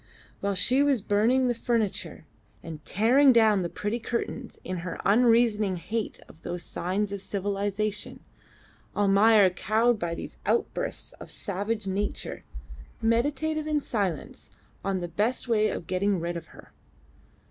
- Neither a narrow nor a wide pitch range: Yes, average, 3.6 semitones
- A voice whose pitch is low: No, high, 210 Hz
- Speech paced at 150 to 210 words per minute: No, average, 140 wpm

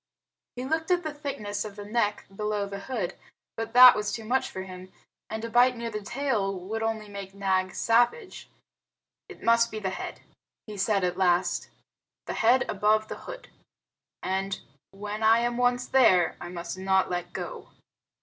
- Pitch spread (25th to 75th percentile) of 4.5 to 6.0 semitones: No, average, 3.7 semitones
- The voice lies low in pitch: No, high, 210 Hz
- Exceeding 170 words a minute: Yes, average, 180 wpm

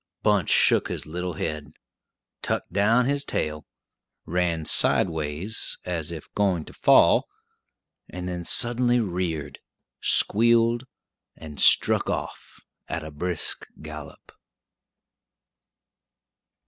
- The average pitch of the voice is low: Yes, very low, 90 Hz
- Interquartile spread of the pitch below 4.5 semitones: No, wide, 5.5 semitones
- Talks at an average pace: No, slow, 100 wpm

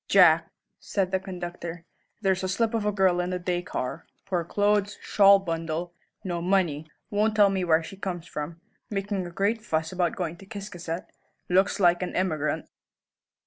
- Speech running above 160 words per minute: Yes, average, 170 wpm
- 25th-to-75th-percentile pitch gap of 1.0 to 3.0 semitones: Yes, narrow, 2.5 semitones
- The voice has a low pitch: No, medium, 185 Hz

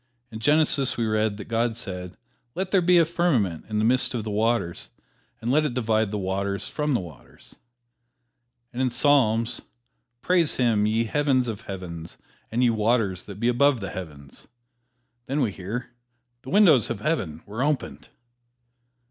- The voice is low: Yes, low, 115 Hz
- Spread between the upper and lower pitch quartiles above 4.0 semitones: Yes, average, 5.0 semitones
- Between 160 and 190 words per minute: Yes, average, 165 wpm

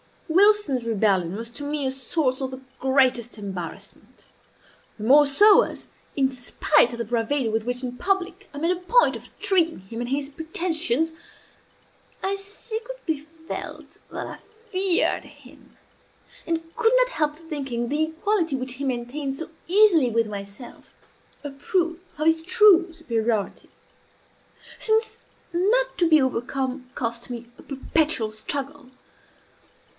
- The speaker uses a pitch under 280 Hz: No, very high, 290 Hz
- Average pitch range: No, wide, 6.1 semitones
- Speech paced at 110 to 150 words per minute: Yes, average, 140 wpm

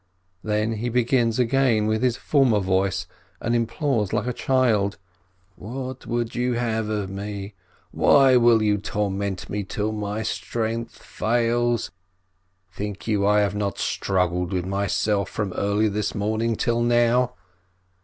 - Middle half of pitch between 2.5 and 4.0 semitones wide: Yes, average, 2.8 semitones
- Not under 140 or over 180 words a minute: Yes, average, 145 wpm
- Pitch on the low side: Yes, low, 110 Hz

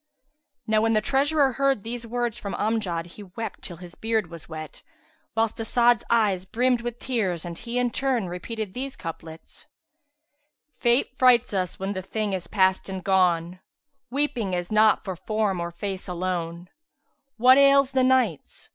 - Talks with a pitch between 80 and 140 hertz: No, high, 215 Hz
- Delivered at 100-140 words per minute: No, average, 165 wpm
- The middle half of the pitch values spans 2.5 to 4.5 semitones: No, average, 5.0 semitones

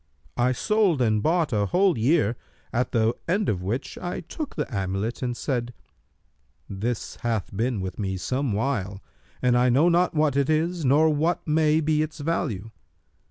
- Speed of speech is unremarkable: Yes, average, 170 wpm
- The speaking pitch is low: Yes, low, 130 Hz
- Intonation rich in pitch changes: Yes, wide, 6.2 semitones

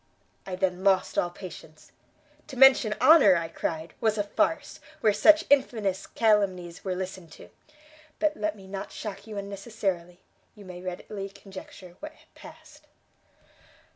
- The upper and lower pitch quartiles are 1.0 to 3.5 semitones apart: Yes, average, 2.8 semitones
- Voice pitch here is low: No, high, 195 Hz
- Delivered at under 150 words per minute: Yes, average, 140 wpm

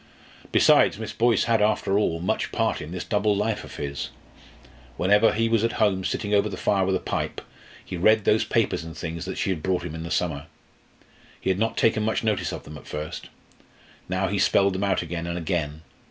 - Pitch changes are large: No, average, 4.0 semitones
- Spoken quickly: Yes, fast, 210 wpm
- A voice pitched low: Yes, very low, 95 Hz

